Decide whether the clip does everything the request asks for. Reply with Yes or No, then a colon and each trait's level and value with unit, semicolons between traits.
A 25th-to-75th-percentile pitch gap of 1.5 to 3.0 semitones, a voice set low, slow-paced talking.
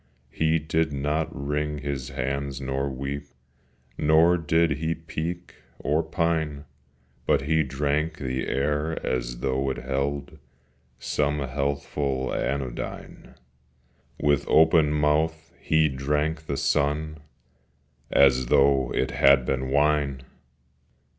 Yes: narrow, 2.5 semitones; very low, 70 Hz; slow, 110 wpm